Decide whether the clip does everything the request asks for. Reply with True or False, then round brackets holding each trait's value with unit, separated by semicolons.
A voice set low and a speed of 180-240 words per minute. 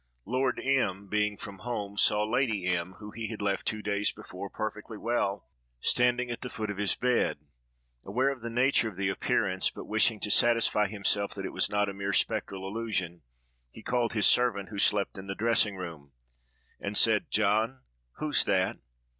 True (105 Hz; 185 wpm)